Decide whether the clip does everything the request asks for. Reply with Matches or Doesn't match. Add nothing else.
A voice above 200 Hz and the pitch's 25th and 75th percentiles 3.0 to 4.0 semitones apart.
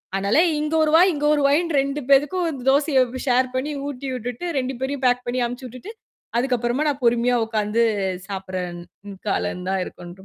Matches